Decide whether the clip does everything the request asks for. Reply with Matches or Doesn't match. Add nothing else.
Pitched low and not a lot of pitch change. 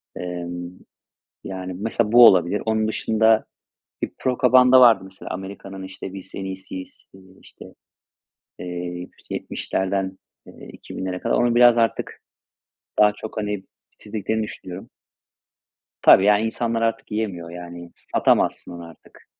Doesn't match